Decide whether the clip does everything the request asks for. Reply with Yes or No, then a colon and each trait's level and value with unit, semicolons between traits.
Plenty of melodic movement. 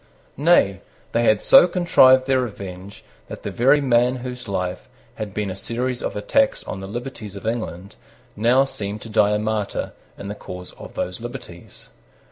No: average, 4.1 semitones